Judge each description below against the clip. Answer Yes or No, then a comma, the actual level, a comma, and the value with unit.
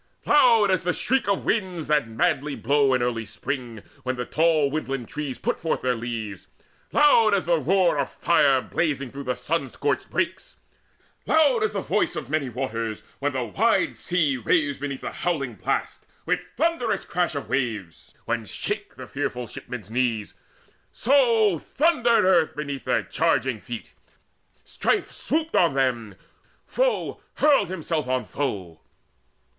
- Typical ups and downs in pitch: No, wide, 7.0 semitones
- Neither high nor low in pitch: Yes, medium, 145 Hz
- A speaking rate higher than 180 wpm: No, average, 150 wpm